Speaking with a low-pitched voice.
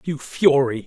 No: medium, 145 Hz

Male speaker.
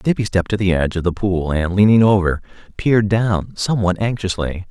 Yes: male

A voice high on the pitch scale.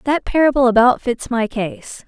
Yes: high, 245 Hz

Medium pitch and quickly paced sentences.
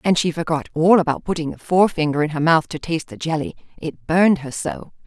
Yes: medium, 160 Hz; fast, 225 wpm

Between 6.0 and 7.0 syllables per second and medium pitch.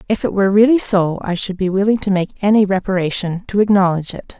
No: 6.5 syllables/s; high, 195 Hz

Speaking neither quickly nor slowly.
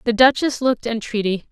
Yes: average, 160 wpm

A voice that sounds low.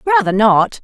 No: high, 240 Hz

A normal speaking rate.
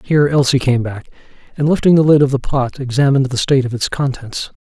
No: fast, 220 wpm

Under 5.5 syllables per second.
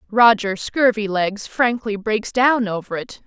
Yes: 4.0 syllables/s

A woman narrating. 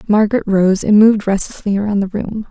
Yes: female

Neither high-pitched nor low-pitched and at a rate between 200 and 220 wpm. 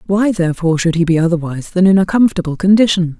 Yes: medium, 180 Hz; fast, 205 wpm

